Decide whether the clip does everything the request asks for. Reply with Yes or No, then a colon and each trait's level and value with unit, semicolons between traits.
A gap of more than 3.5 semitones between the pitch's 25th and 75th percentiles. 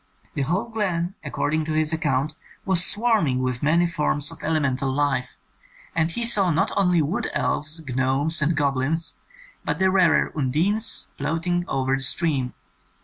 Yes: average, 4.2 semitones